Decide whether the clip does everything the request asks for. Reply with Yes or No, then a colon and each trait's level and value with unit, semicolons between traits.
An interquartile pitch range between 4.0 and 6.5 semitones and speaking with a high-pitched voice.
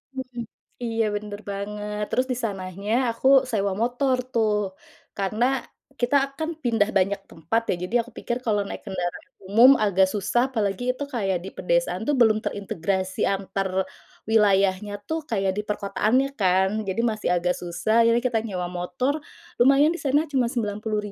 No: average, 3.6 semitones; high, 210 Hz